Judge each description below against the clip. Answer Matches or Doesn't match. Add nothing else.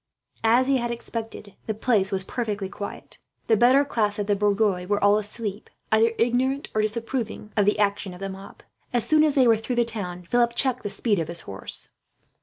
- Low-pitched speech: Doesn't match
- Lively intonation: Doesn't match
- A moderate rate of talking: Doesn't match